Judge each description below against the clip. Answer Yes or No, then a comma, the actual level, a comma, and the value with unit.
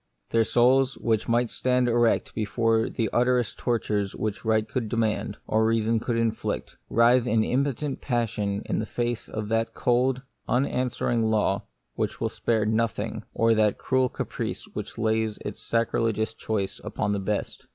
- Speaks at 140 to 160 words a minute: Yes, average, 155 wpm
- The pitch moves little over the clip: Yes, narrow, 1.8 semitones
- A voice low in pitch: Yes, low, 115 Hz